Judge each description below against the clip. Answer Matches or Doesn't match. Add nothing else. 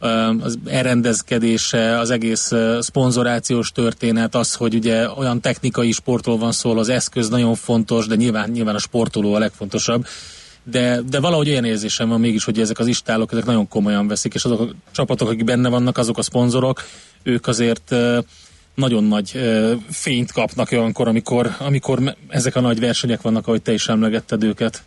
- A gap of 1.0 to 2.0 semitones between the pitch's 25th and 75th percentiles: Matches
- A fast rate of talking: Matches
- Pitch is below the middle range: Matches